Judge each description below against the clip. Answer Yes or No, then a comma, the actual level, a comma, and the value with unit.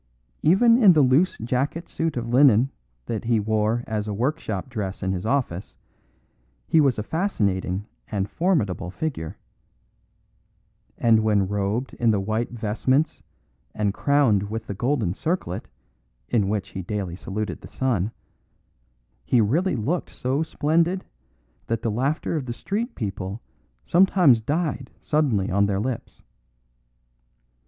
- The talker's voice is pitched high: No, low, 115 Hz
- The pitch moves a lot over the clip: Yes, wide, 6.2 semitones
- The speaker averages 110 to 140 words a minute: Yes, slow, 135 wpm